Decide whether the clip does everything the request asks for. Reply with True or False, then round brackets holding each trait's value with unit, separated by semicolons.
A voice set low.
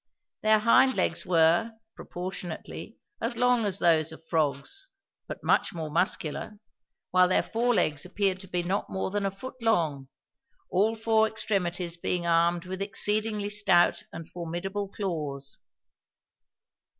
False (185 Hz)